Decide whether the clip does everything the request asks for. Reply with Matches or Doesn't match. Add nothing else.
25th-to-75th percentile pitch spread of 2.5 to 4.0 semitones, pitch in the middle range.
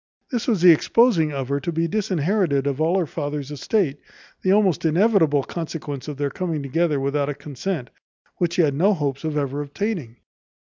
Doesn't match